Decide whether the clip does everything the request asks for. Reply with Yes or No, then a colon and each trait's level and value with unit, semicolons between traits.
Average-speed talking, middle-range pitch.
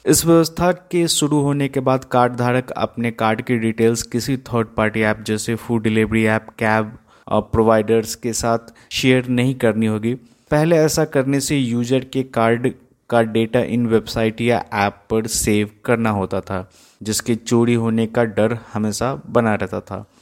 No: average, 170 wpm; low, 115 Hz